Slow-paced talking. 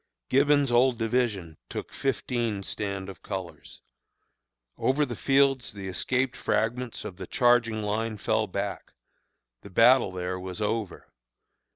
Yes: slow, 130 wpm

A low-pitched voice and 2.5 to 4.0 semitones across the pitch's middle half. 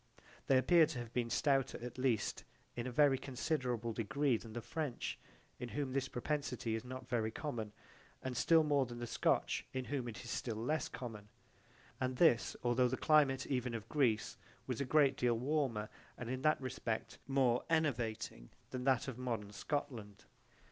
Yes: low, 125 Hz; average, 2.9 semitones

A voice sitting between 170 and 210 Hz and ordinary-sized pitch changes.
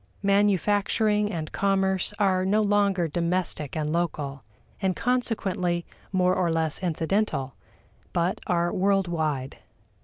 Yes: medium, 185 Hz; average, 3.3 semitones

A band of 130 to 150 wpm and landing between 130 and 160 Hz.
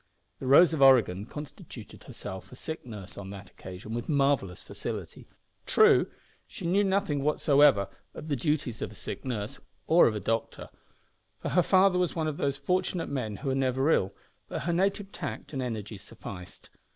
No: average, 175 wpm; low, 135 Hz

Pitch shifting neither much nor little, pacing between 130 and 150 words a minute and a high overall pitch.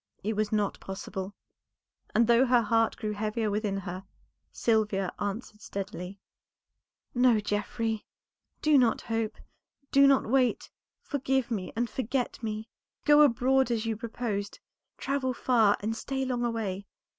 Yes: average, 3.2 semitones; slow, 135 wpm; high, 225 Hz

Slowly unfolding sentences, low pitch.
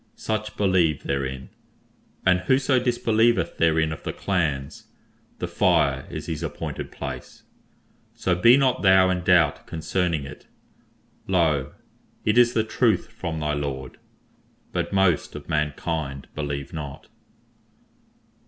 Yes: slow, 125 wpm; very low, 85 Hz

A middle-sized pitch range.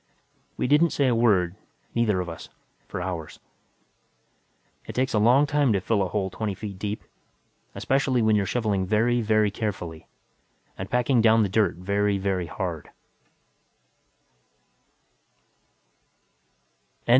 Yes: average, 3.9 semitones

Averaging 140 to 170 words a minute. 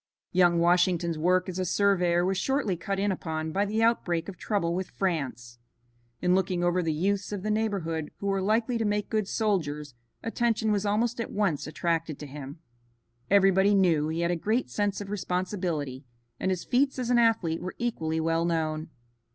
No: average, 185 wpm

